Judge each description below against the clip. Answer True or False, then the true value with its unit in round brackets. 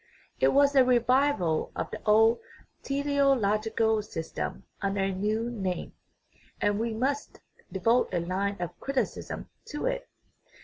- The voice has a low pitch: False (225 Hz)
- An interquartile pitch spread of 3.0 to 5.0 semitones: False (5.5 semitones)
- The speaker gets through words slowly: True (130 wpm)